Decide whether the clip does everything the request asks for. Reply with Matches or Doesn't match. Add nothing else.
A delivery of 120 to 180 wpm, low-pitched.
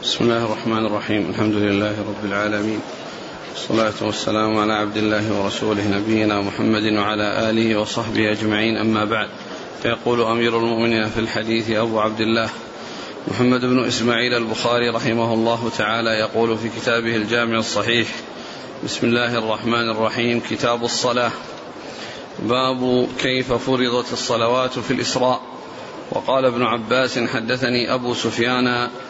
Matches